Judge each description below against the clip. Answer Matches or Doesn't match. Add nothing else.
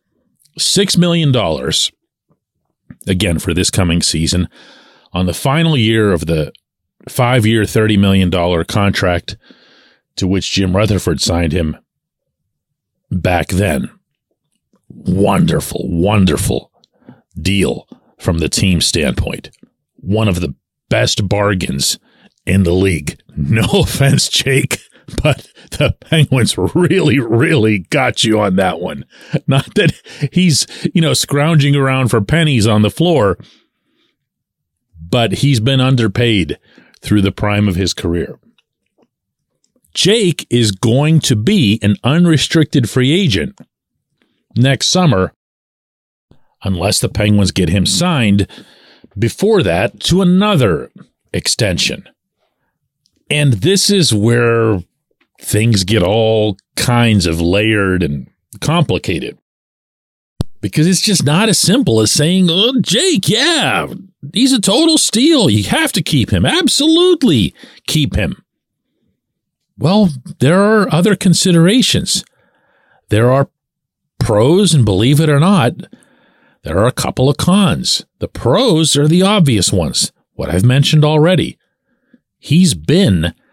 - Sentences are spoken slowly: Matches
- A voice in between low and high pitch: Doesn't match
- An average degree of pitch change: Doesn't match